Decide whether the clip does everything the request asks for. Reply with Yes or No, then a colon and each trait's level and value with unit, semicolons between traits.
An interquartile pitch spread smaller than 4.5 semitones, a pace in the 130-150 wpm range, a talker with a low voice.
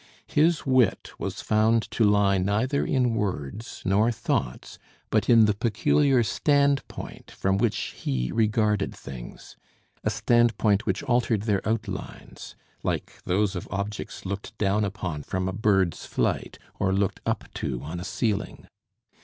Yes: average, 3.3 semitones; average, 140 wpm; low, 105 Hz